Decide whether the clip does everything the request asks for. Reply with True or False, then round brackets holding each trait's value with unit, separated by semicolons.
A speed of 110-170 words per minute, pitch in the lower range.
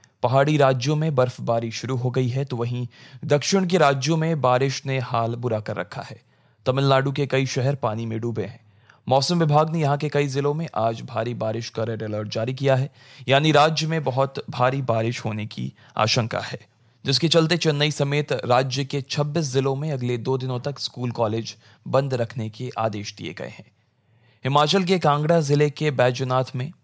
False (190 wpm; 130 Hz)